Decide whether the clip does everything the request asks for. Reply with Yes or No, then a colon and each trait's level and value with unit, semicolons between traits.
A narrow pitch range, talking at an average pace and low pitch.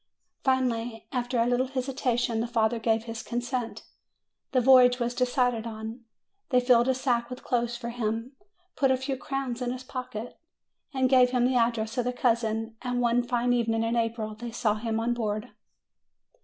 No: narrow, 1.7 semitones; average, 180 wpm; high, 240 Hz